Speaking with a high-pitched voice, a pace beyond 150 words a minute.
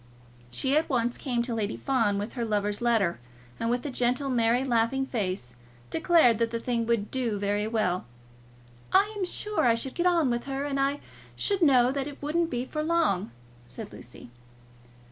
Yes: high, 245 Hz; average, 185 wpm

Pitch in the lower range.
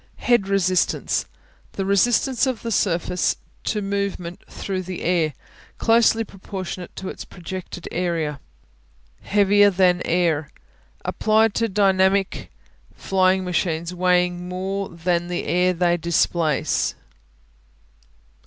No: medium, 185 Hz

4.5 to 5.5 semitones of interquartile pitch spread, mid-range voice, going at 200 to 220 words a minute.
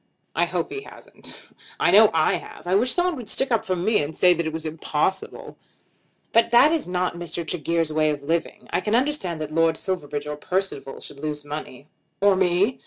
Yes: average, 5.0 semitones; medium, 175 Hz; fast, 205 wpm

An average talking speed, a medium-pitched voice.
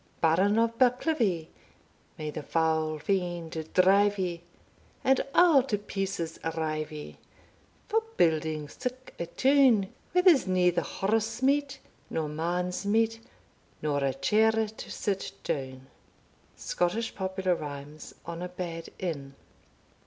No: slow, 125 wpm; medium, 180 Hz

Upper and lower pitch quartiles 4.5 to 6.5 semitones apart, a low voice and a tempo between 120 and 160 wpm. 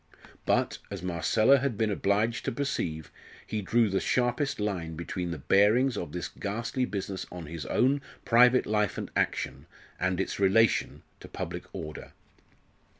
Yes: average, 4.8 semitones; low, 105 Hz; average, 150 wpm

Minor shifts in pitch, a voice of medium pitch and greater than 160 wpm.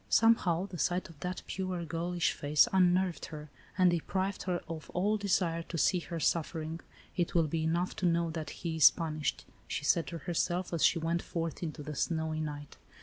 Yes: narrow, 2.1 semitones; medium, 170 Hz; average, 200 wpm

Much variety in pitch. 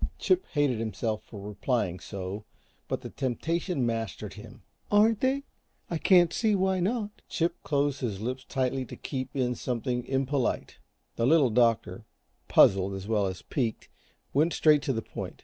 Yes: wide, 6.5 semitones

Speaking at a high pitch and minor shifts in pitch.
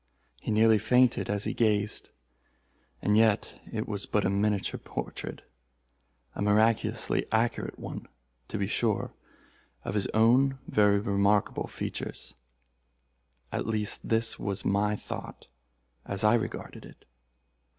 No: low, 105 Hz; narrow, 1.9 semitones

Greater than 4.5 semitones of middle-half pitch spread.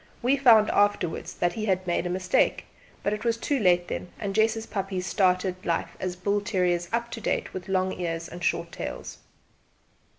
No: average, 3.3 semitones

